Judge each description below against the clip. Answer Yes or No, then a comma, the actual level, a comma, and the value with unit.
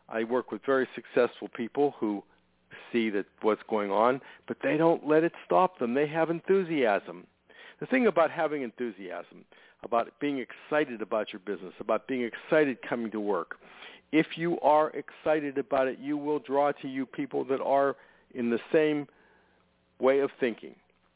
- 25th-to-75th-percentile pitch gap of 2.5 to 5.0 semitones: Yes, average, 4.2 semitones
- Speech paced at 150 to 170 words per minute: Yes, average, 165 wpm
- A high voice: No, medium, 140 Hz